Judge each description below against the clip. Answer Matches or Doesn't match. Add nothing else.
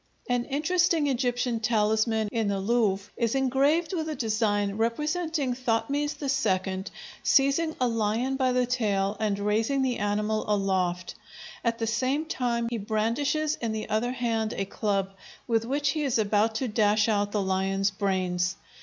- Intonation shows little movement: Doesn't match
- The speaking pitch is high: Matches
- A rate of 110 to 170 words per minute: Matches